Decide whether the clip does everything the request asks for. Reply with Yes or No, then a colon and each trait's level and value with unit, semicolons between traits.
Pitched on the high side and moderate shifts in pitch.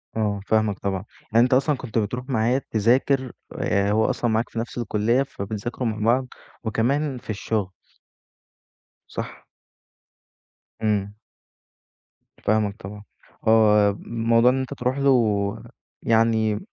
No: low, 115 Hz; average, 3.0 semitones